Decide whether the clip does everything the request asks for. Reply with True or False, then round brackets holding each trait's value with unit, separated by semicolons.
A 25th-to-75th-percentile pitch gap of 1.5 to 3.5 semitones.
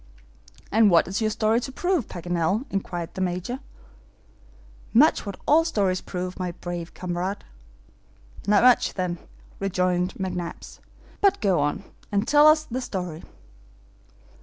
False (4.5 semitones)